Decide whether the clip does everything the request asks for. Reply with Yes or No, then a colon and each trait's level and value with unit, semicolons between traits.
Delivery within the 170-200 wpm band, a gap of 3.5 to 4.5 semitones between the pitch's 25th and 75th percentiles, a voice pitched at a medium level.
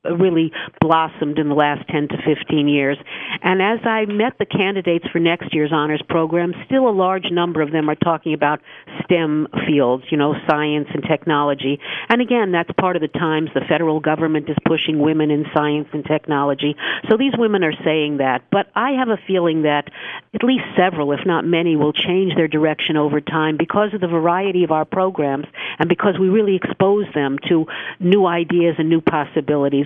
Yes: average, 195 wpm; average, 3.8 semitones; medium, 160 Hz